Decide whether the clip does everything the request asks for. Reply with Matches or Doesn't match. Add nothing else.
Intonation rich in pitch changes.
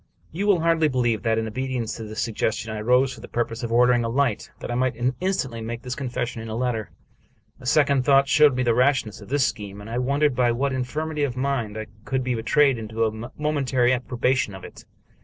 Doesn't match